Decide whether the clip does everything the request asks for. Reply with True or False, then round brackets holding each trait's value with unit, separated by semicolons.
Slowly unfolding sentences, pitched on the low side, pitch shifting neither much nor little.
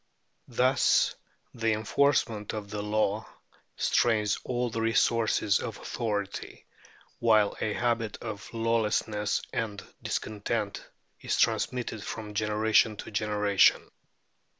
False (105 wpm; 110 Hz; 1.7 semitones)